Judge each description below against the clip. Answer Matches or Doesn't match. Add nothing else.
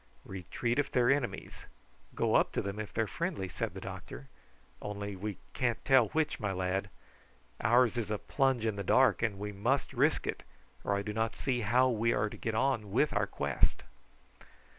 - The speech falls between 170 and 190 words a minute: Doesn't match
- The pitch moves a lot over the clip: Doesn't match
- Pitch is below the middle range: Matches